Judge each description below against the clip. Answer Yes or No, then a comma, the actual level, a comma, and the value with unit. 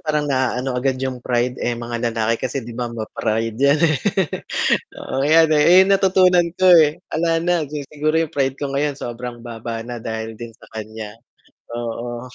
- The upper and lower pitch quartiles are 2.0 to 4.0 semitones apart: No, average, 4.4 semitones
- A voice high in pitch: No, low, 125 Hz